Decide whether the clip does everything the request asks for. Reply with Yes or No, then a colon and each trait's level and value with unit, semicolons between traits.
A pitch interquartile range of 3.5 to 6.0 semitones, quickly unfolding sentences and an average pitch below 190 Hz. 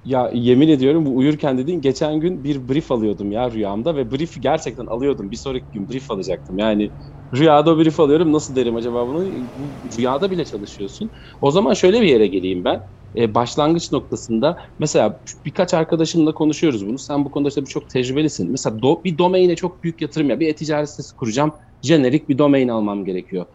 Yes: average, 4.5 semitones; fast, 185 wpm; medium, 140 Hz